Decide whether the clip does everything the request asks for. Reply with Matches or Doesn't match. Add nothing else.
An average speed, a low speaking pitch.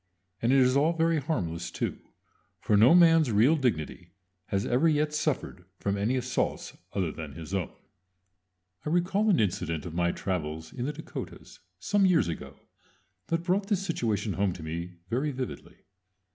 Matches